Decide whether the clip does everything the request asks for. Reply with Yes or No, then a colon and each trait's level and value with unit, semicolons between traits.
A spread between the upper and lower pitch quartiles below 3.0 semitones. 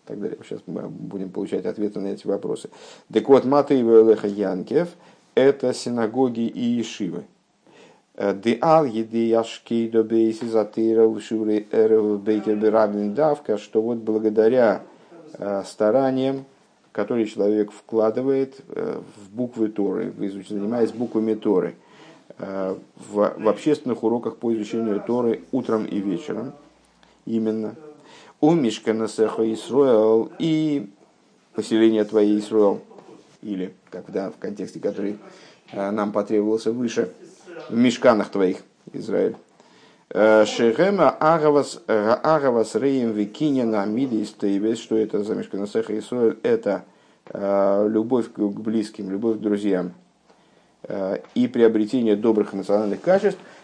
Yes: narrow, 2.6 semitones